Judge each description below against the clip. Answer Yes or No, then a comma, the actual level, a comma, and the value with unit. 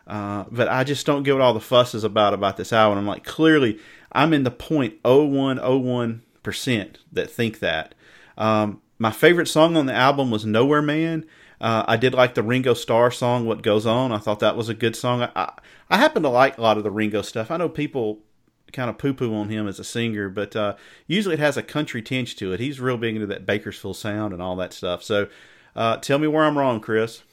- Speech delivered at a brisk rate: Yes, fast, 230 wpm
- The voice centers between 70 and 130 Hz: Yes, low, 115 Hz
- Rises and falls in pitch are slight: No, average, 3.5 semitones